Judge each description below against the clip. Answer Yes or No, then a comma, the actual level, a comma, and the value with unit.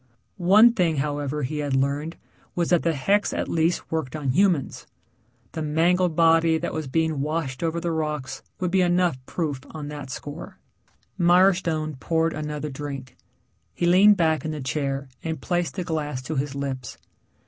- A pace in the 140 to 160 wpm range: No, average, 170 wpm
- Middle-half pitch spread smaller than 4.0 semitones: Yes, average, 3.1 semitones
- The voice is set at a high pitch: No, medium, 155 Hz